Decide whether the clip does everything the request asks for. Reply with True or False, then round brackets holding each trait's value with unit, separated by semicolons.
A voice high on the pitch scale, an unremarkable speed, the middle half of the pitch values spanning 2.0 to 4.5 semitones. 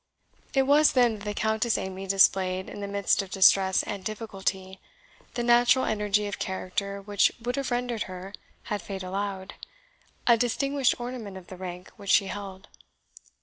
True (200 Hz; 165 wpm; 3.8 semitones)